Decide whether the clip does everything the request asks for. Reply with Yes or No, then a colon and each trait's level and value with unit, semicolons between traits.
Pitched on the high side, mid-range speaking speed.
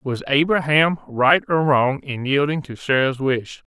No: medium, 140 Hz; average, 160 wpm